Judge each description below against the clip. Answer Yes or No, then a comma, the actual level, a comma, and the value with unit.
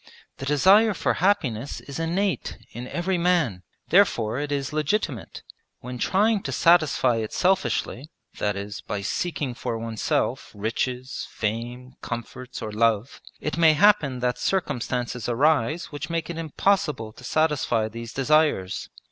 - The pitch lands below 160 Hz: Yes, low, 135 Hz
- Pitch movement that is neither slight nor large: No, wide, 6.2 semitones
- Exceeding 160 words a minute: No, average, 140 wpm